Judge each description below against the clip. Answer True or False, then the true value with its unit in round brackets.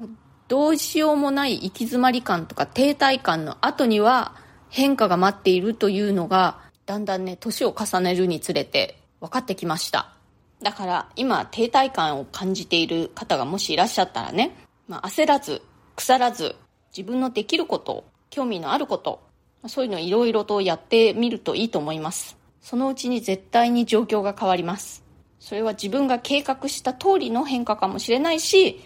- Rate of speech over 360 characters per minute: False (350 characters per minute)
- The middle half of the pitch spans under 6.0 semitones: True (5.6 semitones)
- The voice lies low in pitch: False (225 Hz)